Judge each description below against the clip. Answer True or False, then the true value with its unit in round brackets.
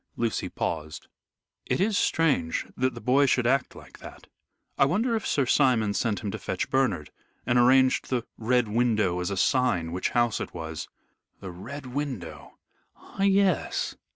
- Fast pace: False (165 wpm)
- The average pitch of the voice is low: True (125 Hz)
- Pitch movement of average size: False (6.1 semitones)